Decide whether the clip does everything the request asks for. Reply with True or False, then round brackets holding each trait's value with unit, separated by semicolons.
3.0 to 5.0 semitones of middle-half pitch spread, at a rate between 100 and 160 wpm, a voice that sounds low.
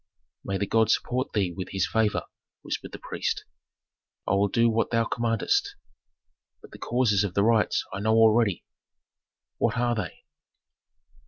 False (2.6 semitones; 155 wpm; 110 Hz)